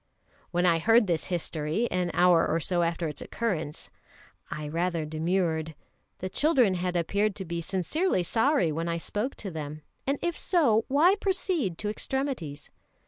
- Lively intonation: Yes, wide, 5.8 semitones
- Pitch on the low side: No, medium, 180 Hz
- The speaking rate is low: No, average, 160 wpm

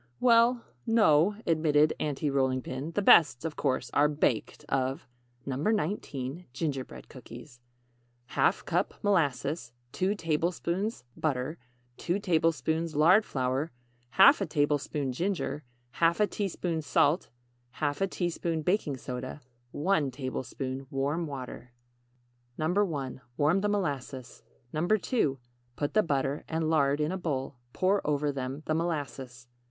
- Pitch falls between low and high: Yes, medium, 150 Hz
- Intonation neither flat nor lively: Yes, average, 4.4 semitones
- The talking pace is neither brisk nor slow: No, slow, 120 wpm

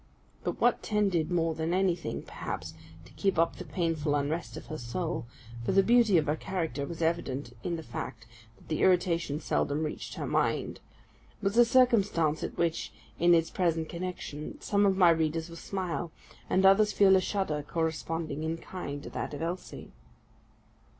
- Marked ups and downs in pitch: No, average, 3.3 semitones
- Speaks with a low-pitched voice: No, medium, 170 Hz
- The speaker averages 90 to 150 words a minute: No, average, 175 wpm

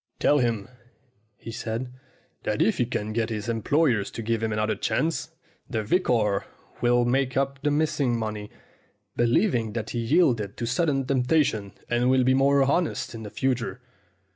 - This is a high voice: No, low, 120 Hz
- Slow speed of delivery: No, average, 165 wpm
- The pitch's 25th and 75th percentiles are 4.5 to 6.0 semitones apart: No, average, 3.6 semitones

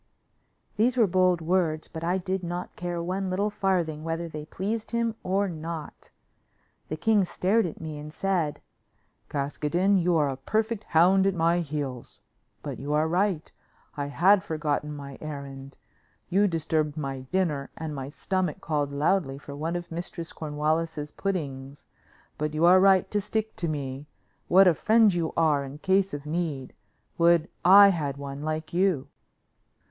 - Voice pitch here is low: No, medium, 165 Hz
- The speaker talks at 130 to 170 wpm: Yes, average, 165 wpm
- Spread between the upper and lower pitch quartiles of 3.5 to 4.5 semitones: Yes, average, 4.1 semitones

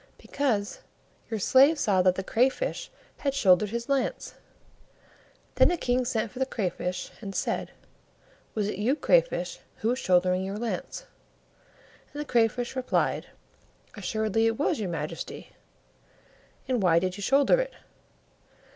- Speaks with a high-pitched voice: Yes, high, 225 Hz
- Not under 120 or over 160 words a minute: Yes, average, 140 wpm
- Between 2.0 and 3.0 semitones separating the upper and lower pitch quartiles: No, average, 5.3 semitones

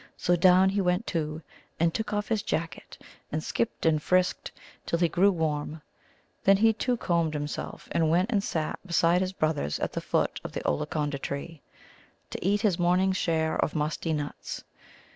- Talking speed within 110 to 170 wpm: No, average, 180 wpm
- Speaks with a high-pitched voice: No, medium, 170 Hz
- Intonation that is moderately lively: Yes, average, 3.5 semitones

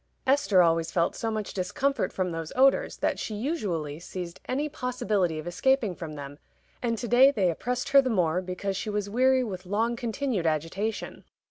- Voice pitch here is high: Yes, high, 205 Hz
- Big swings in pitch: Yes, wide, 6.3 semitones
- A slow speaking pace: No, average, 185 wpm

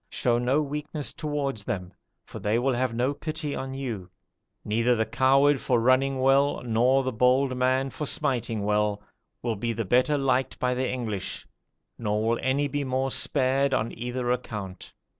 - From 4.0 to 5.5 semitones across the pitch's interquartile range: No, average, 2.9 semitones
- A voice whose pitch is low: Yes, low, 130 Hz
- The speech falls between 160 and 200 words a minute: Yes, average, 175 wpm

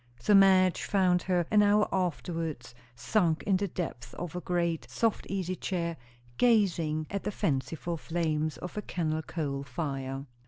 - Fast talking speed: No, average, 155 wpm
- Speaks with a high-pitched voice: No, medium, 170 Hz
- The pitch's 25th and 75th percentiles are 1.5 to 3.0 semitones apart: No, average, 3.6 semitones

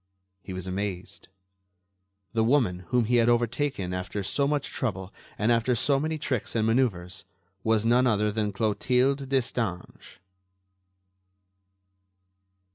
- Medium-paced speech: No, slow, 120 wpm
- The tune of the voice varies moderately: Yes, average, 4.4 semitones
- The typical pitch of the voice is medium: No, low, 115 Hz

